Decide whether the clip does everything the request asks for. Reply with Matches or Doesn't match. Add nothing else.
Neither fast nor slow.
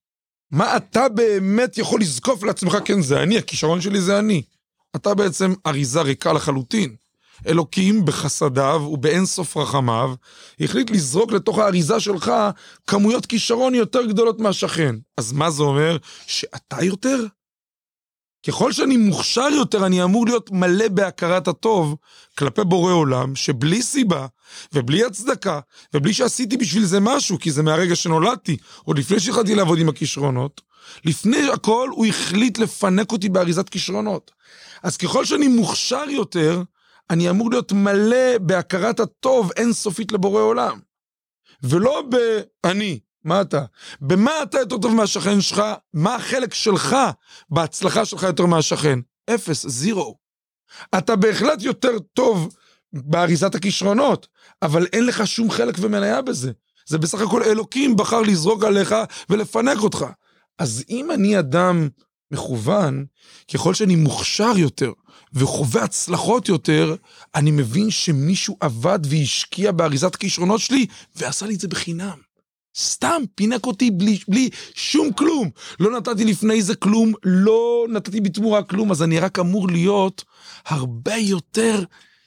Matches